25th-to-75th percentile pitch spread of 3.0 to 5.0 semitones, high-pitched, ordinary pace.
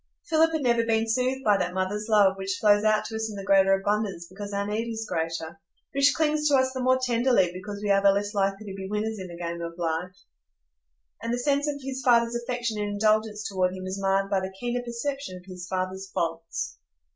No: average, 3.9 semitones; high, 205 Hz; fast, 225 wpm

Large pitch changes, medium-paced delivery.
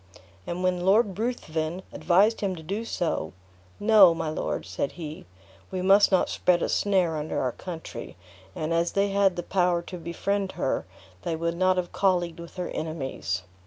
No: average, 2.9 semitones; average, 175 wpm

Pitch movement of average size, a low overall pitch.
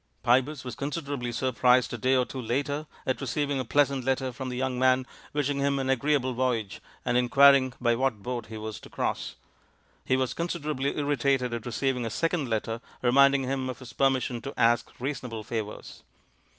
No: narrow, 2.2 semitones; low, 130 Hz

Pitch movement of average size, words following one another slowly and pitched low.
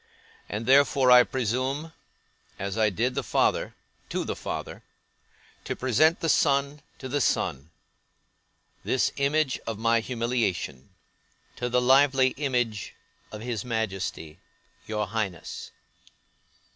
Yes: average, 3.8 semitones; slow, 120 wpm; low, 125 Hz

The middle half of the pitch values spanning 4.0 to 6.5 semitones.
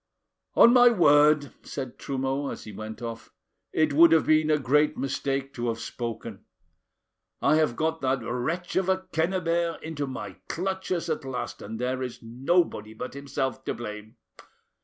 Yes: average, 4.8 semitones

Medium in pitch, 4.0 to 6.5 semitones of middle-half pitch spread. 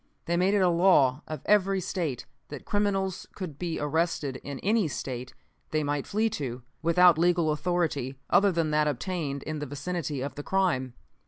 Yes: medium, 160 Hz; average, 4.3 semitones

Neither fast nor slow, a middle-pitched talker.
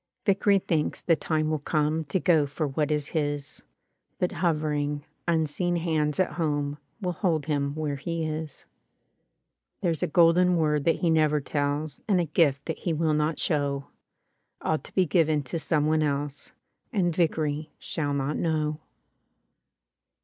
Yes: average, 160 wpm; medium, 155 Hz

